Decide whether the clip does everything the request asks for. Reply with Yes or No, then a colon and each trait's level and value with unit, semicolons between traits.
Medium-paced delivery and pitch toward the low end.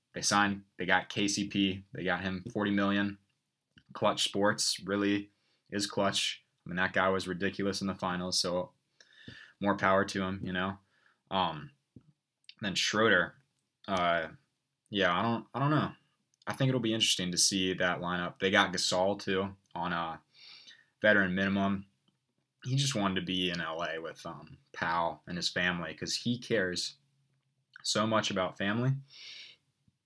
Yes: average, 155 wpm; low, 100 Hz